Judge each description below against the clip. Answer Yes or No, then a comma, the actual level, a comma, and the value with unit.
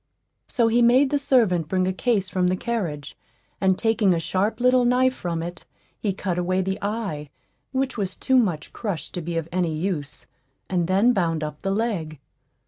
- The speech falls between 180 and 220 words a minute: Yes, average, 190 wpm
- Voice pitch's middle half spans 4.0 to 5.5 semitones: Yes, average, 5.2 semitones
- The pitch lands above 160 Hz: Yes, high, 190 Hz